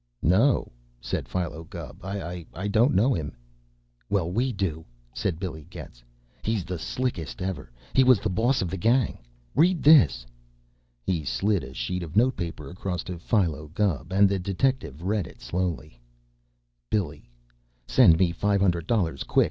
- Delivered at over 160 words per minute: No, average, 155 wpm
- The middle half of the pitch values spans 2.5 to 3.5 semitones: No, average, 4.4 semitones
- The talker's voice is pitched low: Yes, very low, 90 Hz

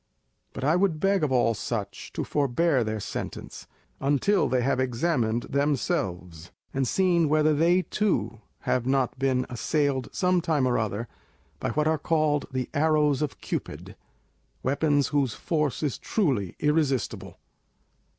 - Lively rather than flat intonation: No, average, 4.1 semitones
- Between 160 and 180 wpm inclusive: No, average, 140 wpm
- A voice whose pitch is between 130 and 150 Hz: Yes, medium, 140 Hz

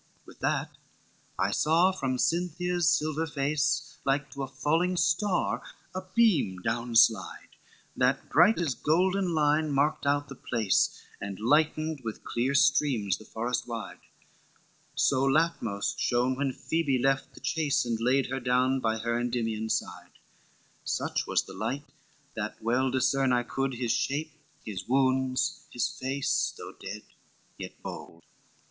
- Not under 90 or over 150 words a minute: Yes, average, 145 wpm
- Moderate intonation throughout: Yes, average, 4.1 semitones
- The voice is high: No, low, 135 Hz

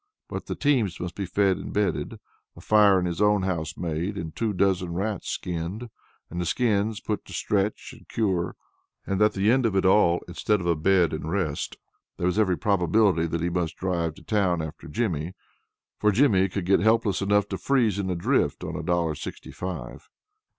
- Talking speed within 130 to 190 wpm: No, average, 200 wpm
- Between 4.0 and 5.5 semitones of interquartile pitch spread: No, average, 3.3 semitones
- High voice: No, very low, 95 Hz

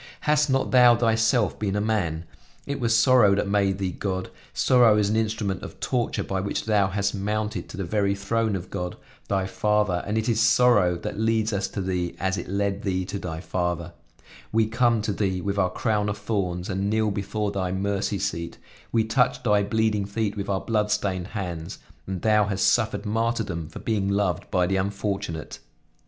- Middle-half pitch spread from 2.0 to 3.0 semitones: Yes, narrow, 2.6 semitones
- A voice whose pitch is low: Yes, low, 100 Hz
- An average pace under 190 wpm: No, average, 195 wpm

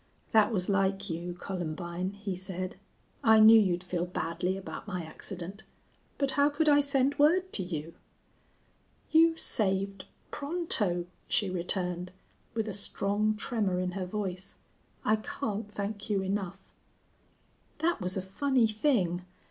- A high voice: Yes, high, 195 Hz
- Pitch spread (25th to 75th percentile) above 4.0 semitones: No, average, 3.5 semitones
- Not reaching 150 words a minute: Yes, average, 140 wpm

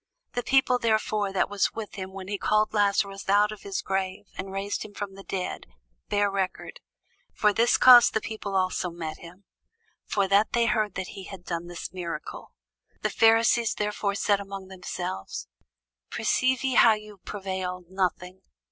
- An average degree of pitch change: No, narrow, 2.2 semitones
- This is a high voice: Yes, high, 200 Hz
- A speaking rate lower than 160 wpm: No, average, 170 wpm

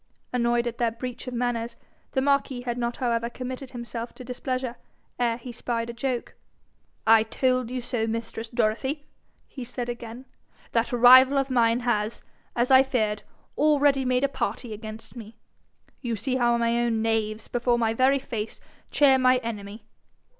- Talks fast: No, average, 165 wpm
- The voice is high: Yes, high, 240 Hz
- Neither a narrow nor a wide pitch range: No, narrow, 1.9 semitones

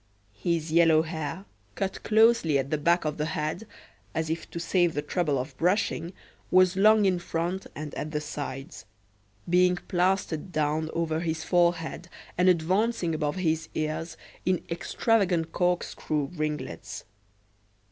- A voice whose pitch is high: No, medium, 165 Hz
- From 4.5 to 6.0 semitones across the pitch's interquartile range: No, average, 2.8 semitones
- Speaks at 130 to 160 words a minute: Yes, average, 140 wpm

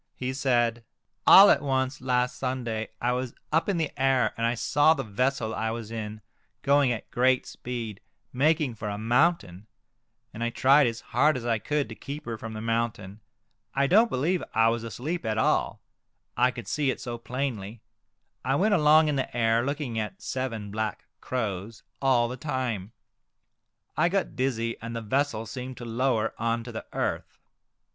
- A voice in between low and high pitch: No, low, 125 Hz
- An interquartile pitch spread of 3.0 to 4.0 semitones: Yes, average, 3.4 semitones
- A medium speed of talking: Yes, average, 185 wpm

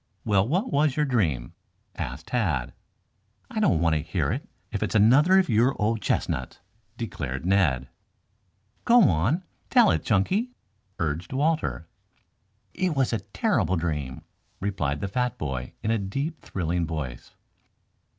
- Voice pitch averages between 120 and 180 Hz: No, low, 100 Hz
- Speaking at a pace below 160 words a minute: Yes, average, 145 wpm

